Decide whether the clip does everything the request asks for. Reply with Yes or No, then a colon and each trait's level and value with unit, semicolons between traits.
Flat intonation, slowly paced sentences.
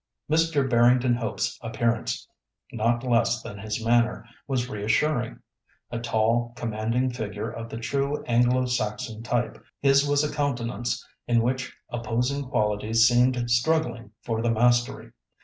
Yes: narrow, 2.0 semitones; slow, 130 wpm